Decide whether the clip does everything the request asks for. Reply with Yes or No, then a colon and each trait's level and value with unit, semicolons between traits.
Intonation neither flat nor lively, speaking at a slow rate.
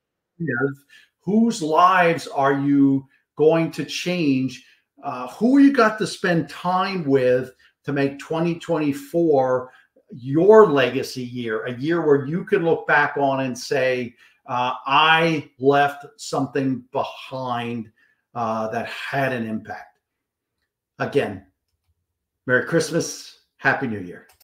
Yes: average, 4.5 semitones; slow, 120 wpm